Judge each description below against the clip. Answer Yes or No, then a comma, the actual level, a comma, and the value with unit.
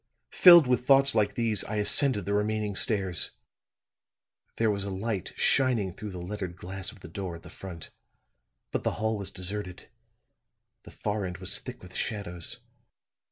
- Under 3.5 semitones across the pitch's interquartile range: Yes, average, 2.9 semitones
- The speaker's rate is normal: Yes, average, 165 wpm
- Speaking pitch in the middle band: No, low, 100 Hz